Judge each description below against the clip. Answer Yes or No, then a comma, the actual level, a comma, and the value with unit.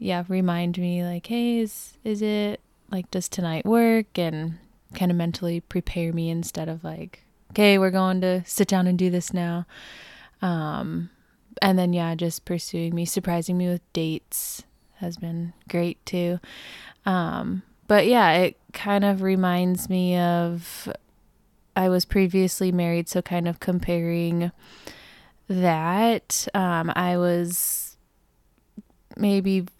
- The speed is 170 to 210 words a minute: No, slow, 135 wpm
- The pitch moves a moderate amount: No, narrow, 2.3 semitones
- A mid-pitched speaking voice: Yes, medium, 180 Hz